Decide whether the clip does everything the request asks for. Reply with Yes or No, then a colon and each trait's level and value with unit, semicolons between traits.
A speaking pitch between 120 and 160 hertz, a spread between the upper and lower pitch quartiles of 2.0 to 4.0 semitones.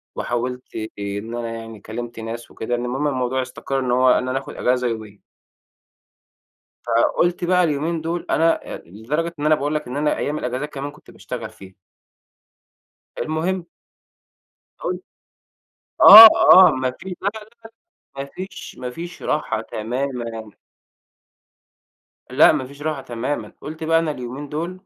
No: low, 135 Hz; average, 4.6 semitones